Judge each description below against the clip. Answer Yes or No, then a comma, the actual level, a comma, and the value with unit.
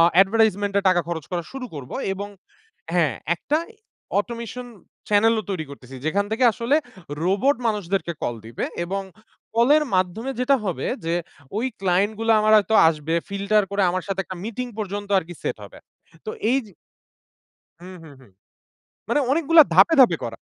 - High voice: Yes, high, 200 Hz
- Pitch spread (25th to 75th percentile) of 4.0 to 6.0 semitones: Yes, average, 4.5 semitones